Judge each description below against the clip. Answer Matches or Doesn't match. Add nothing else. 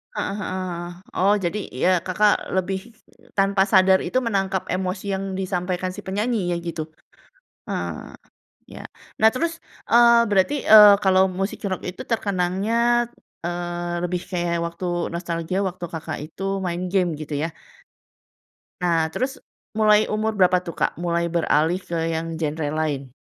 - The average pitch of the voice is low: Doesn't match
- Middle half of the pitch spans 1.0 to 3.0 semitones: Matches